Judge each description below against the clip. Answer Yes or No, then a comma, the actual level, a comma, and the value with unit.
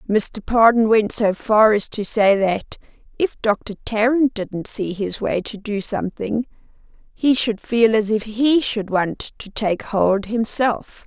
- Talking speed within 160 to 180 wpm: Yes, average, 170 wpm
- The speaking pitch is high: Yes, high, 215 Hz